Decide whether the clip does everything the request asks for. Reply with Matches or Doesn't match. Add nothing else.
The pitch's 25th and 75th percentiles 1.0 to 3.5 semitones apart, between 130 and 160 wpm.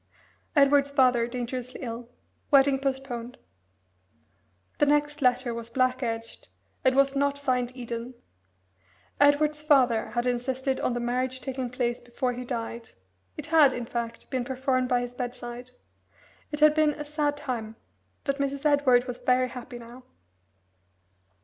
Matches